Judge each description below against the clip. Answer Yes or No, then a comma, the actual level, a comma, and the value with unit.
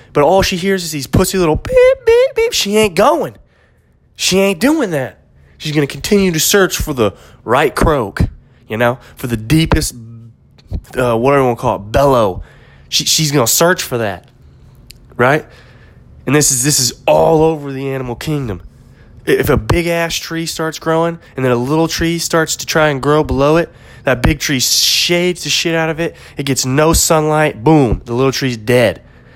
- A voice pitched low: No, medium, 150 Hz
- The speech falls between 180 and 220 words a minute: Yes, average, 195 wpm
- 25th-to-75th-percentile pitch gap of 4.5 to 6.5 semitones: Yes, average, 5.0 semitones